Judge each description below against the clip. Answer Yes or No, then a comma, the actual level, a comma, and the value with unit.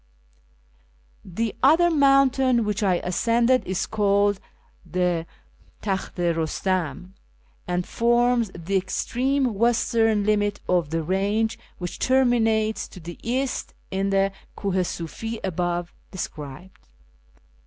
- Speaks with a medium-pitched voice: No, high, 205 Hz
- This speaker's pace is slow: Yes, slow, 110 wpm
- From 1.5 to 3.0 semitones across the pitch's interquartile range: No, average, 4.6 semitones